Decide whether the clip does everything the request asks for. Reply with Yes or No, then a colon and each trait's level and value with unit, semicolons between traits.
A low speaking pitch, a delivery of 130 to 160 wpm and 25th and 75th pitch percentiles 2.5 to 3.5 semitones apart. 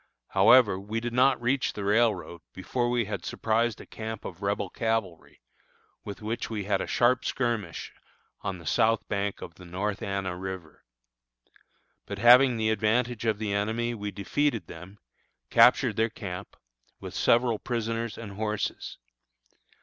Yes: low, 110 Hz; average, 150 wpm; average, 3.0 semitones